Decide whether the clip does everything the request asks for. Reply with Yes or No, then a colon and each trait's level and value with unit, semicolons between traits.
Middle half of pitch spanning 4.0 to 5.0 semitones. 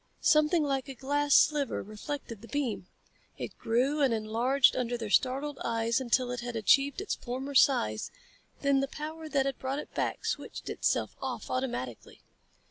No: average, 3.3 semitones